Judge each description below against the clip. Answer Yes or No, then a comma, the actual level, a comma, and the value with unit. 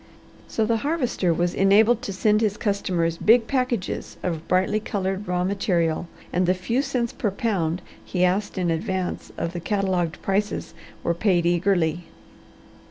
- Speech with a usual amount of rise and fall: Yes, average, 3.4 semitones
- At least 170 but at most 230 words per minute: No, average, 155 wpm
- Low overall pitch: No, high, 190 Hz